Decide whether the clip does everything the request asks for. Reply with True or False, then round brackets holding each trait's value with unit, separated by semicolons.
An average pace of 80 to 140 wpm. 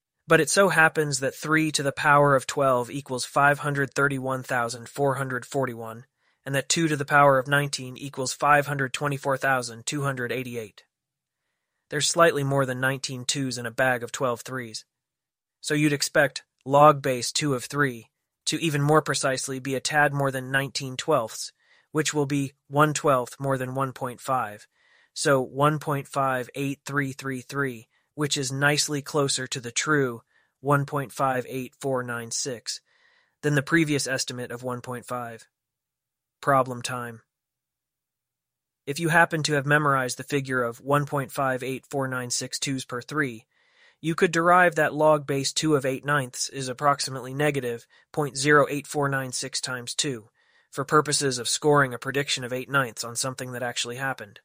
True (135 wpm)